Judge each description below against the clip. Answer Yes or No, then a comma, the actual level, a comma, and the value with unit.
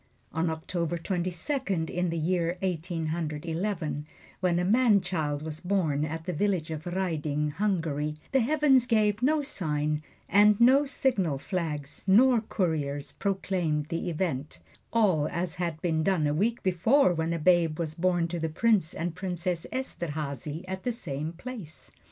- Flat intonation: No, average, 3.9 semitones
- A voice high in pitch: No, medium, 175 Hz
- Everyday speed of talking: Yes, average, 160 wpm